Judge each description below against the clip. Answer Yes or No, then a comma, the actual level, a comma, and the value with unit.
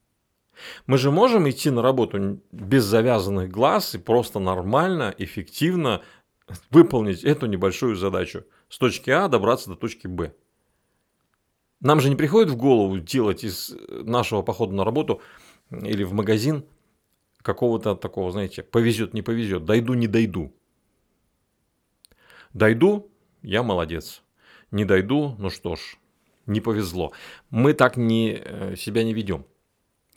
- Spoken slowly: No, average, 125 wpm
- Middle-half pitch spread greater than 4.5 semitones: Yes, average, 5.2 semitones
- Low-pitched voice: Yes, low, 115 Hz